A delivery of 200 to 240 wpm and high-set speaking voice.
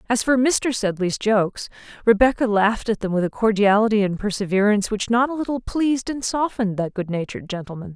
No: average, 180 wpm; high, 215 Hz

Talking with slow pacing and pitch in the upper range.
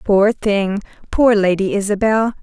Yes: slow, 100 wpm; high, 205 Hz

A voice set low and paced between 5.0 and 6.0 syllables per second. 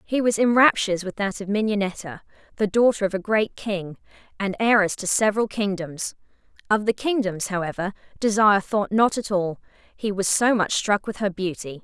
No: high, 200 Hz; 5.3 syllables/s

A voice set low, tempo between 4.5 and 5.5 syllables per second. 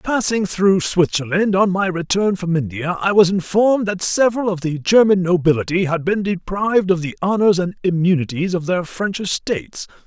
No: medium, 185 Hz; 5.1 syllables/s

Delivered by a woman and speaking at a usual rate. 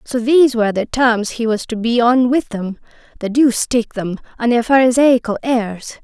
Yes: female; average, 190 wpm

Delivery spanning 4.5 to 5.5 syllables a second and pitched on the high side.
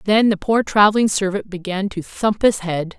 Yes: 4.9 syllables/s; high, 200 Hz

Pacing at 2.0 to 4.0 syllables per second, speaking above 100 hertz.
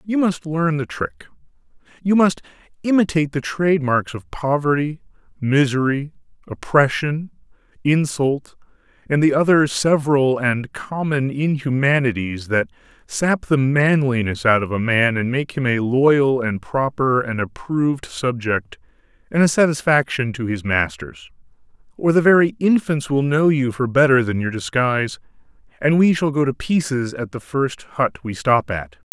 No: 4.5 syllables/s; low, 135 Hz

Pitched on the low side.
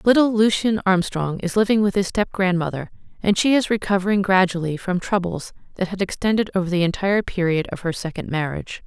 No: high, 190 Hz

